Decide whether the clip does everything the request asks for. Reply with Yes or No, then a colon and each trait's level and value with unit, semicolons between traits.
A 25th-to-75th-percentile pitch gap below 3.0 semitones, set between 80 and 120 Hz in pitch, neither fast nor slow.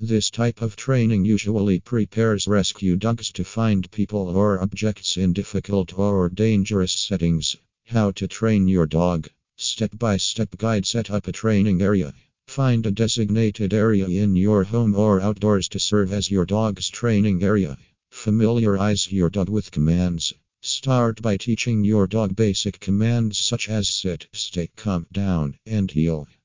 Yes: narrow, 2.6 semitones; low, 100 Hz; average, 155 wpm